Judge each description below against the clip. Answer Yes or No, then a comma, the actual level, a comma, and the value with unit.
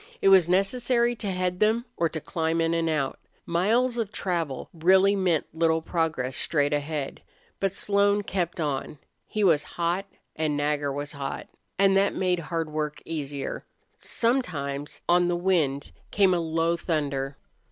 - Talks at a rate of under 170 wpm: Yes, average, 155 wpm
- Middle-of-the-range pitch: Yes, medium, 170 Hz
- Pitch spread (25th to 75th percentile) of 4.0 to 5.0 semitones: Yes, average, 4.4 semitones